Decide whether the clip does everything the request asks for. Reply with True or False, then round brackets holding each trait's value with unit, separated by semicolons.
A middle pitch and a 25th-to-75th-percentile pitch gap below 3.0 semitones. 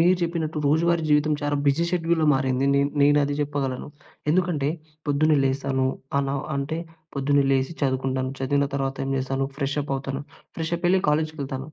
True (145 Hz; 2.6 semitones)